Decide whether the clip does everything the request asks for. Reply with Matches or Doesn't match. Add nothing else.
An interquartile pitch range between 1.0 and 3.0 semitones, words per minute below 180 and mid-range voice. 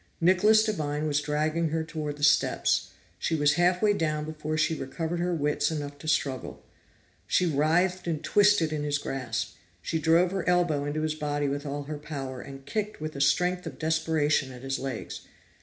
Doesn't match